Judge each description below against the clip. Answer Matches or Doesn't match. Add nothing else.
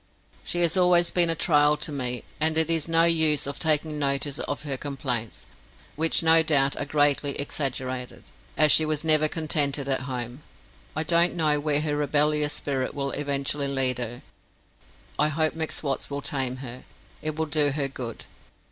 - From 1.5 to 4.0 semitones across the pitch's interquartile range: Matches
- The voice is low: Doesn't match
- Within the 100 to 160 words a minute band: Doesn't match